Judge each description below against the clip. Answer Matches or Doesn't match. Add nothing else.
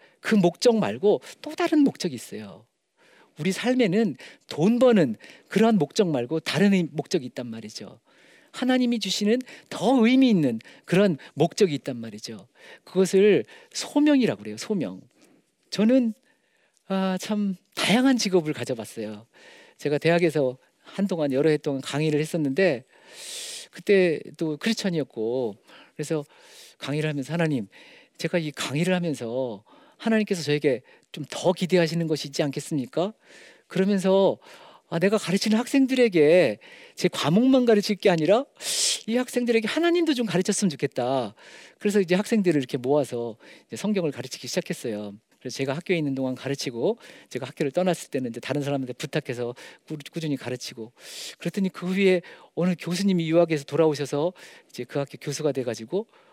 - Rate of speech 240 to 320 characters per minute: Doesn't match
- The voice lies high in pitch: Doesn't match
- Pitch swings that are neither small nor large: Doesn't match